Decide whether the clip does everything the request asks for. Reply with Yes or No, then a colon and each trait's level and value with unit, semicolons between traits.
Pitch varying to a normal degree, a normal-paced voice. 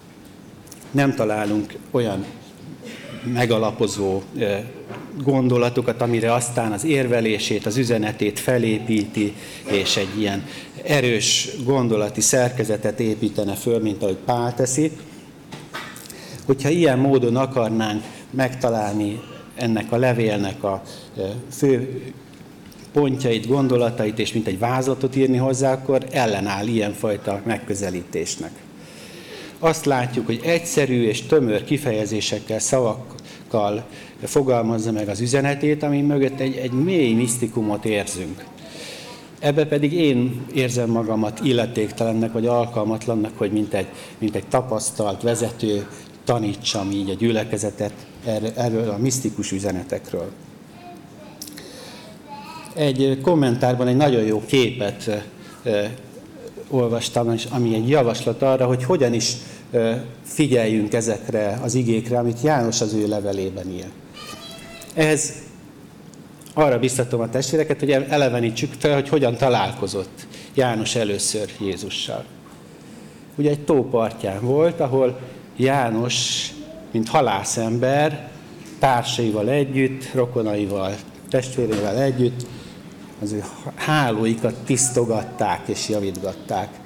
No: average, 3.7 semitones; slow, 100 wpm